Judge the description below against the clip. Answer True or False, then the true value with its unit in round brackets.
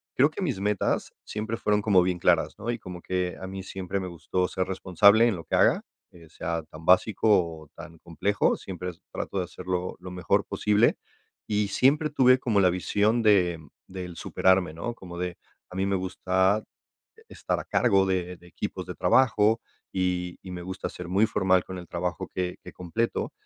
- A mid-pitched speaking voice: False (95 Hz)